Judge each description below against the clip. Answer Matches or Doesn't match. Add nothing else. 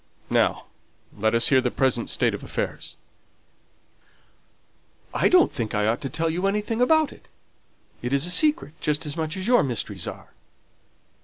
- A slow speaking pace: Doesn't match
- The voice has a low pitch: Doesn't match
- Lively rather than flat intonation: Matches